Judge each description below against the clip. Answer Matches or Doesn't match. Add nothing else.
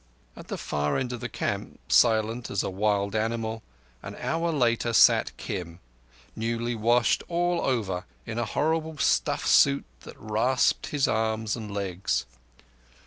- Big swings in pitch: Doesn't match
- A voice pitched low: Matches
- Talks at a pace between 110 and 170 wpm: Matches